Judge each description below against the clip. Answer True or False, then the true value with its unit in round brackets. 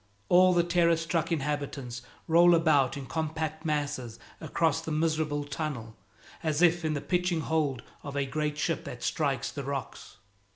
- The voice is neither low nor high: True (155 Hz)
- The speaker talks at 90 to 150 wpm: False (160 wpm)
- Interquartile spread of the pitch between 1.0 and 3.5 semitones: True (2.6 semitones)